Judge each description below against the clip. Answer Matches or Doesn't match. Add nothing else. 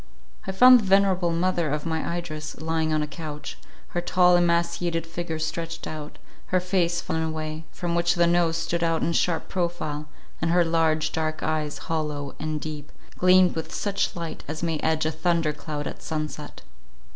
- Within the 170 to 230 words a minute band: Matches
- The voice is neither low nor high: Matches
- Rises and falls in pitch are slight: Matches